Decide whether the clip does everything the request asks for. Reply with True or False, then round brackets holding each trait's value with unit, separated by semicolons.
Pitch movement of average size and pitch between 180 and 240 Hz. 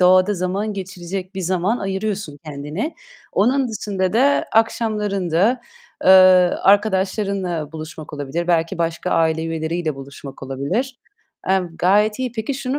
True (4.4 semitones; 185 Hz)